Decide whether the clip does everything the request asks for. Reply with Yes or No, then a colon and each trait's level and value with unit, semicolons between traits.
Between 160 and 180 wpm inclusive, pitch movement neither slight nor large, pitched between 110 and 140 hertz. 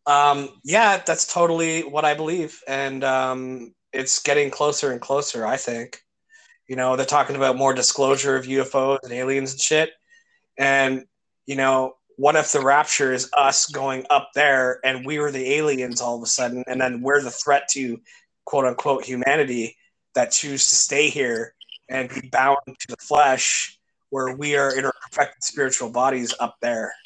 No: average, 175 wpm; narrow, 1.9 semitones; low, 135 Hz